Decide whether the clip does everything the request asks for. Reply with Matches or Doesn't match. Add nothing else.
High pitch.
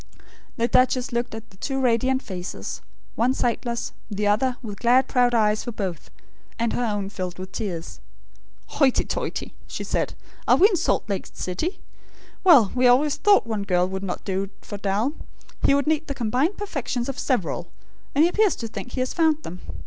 Matches